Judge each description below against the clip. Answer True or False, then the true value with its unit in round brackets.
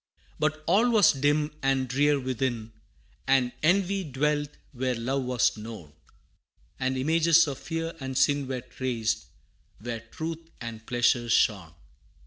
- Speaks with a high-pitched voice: False (130 Hz)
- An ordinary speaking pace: False (130 wpm)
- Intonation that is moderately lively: True (4.1 semitones)